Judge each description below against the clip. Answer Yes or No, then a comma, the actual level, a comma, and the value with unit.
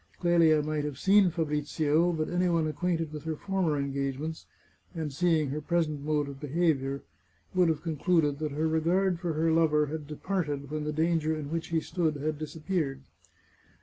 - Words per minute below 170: No, average, 180 wpm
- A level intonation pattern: Yes, narrow, 2.2 semitones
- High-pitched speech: No, medium, 155 Hz